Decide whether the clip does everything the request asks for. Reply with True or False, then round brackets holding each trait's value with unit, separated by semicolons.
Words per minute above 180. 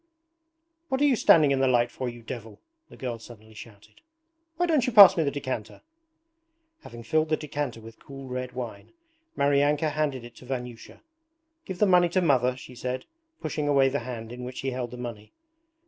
True (195 wpm)